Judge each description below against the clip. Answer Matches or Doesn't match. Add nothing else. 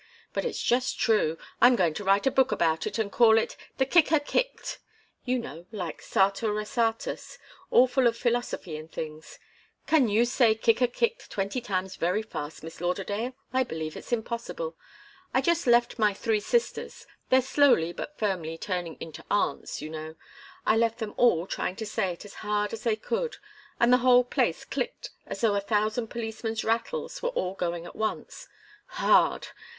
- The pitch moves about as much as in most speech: Matches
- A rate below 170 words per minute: Doesn't match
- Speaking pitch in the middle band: Doesn't match